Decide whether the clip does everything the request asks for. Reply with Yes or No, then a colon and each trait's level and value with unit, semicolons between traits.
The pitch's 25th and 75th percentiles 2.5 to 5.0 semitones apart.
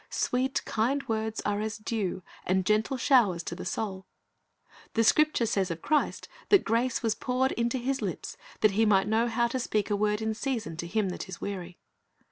Yes: average, 3.4 semitones